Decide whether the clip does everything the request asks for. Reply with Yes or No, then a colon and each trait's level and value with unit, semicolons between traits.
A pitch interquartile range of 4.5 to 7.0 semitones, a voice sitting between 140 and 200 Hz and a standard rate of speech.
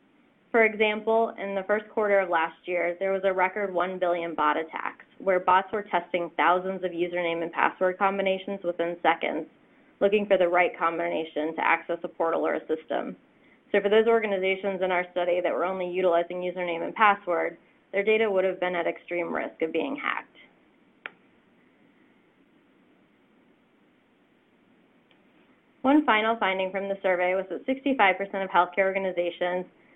No: average, 3.3 semitones; high, 190 Hz; average, 155 wpm